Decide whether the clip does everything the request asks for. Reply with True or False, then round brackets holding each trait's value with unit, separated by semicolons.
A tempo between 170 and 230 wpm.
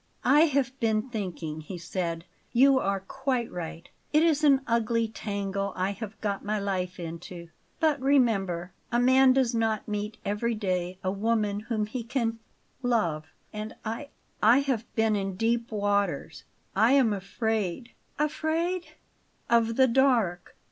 False (155 wpm)